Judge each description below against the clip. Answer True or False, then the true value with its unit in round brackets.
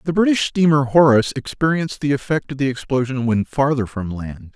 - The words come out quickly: False (185 wpm)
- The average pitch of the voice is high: False (135 Hz)